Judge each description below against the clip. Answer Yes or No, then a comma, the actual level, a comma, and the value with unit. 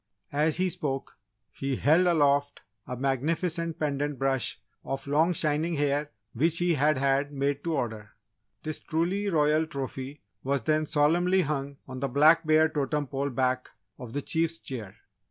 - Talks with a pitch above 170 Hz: No, medium, 145 Hz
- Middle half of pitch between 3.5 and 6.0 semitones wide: No, average, 2.8 semitones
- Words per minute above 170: No, average, 155 wpm